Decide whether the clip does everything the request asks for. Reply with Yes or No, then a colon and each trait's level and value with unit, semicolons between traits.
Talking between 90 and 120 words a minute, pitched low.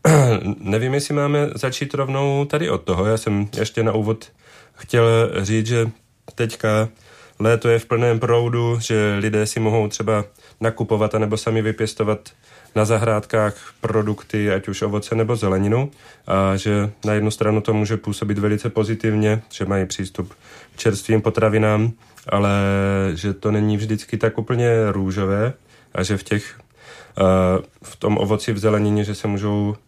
No: average, 150 wpm; low, 110 Hz